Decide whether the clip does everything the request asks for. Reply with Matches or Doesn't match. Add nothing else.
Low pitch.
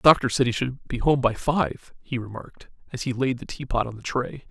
Matches